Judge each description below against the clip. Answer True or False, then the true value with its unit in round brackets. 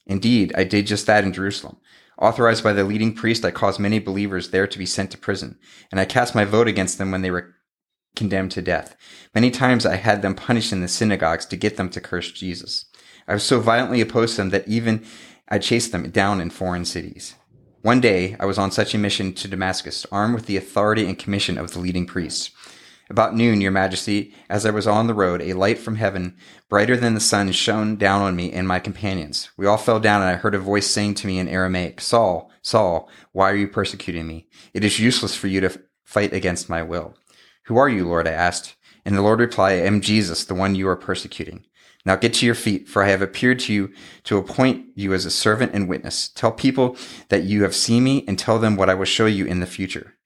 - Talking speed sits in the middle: False (235 wpm)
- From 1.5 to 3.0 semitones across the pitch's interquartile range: True (2.5 semitones)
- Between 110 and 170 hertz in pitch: False (100 Hz)